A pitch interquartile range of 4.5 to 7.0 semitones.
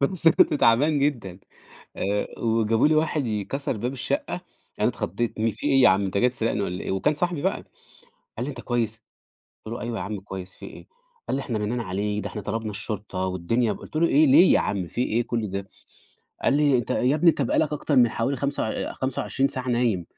Yes: average, 4.9 semitones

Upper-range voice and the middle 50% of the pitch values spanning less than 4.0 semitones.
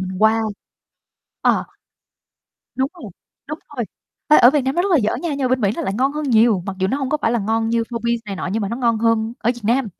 Yes: high, 235 Hz; average, 3.4 semitones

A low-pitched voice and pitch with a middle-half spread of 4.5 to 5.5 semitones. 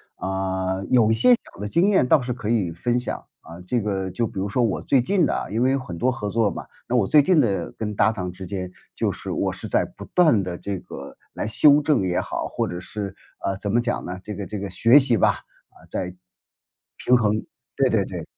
Yes: low, 105 Hz; average, 4.8 semitones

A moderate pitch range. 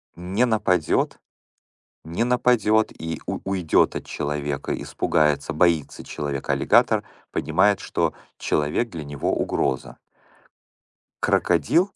No: wide, 6.5 semitones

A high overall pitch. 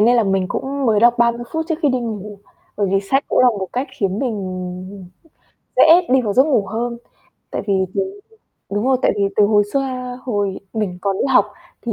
Yes: high, 220 Hz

